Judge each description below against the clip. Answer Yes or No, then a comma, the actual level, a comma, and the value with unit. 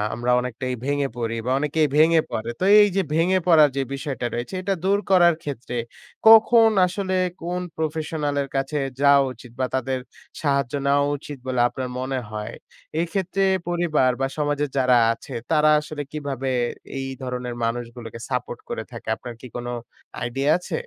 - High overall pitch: No, medium, 140 Hz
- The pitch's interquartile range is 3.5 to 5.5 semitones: Yes, average, 4.1 semitones